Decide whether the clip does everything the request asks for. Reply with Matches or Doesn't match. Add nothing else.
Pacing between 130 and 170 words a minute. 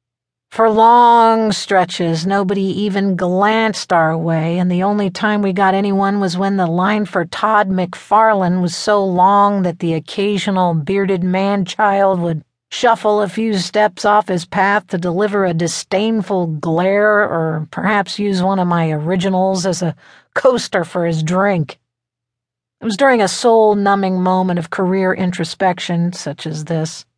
Matches